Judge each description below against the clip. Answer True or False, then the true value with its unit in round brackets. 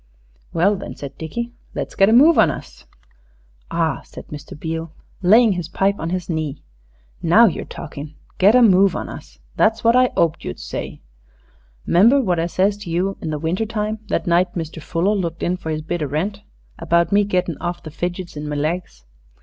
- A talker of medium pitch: True (175 Hz)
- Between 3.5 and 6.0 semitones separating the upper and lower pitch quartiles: True (4.1 semitones)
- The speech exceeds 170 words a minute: True (200 wpm)